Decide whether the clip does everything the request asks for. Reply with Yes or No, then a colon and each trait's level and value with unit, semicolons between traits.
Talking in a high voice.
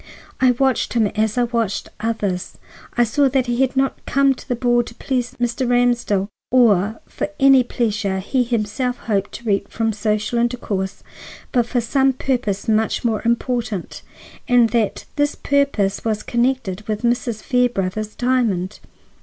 Yes: high, 235 Hz